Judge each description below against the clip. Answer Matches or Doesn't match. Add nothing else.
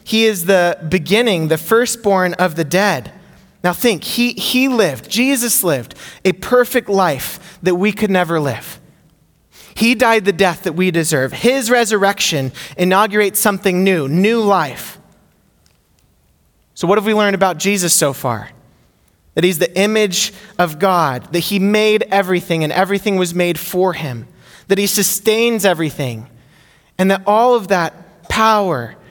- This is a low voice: Doesn't match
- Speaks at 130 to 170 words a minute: Matches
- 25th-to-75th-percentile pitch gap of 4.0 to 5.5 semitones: Matches